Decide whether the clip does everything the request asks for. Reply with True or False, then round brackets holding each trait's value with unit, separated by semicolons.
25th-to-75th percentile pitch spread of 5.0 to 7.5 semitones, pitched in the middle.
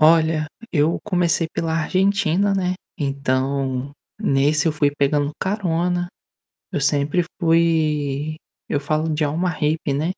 False (3.0 semitones; 155 Hz)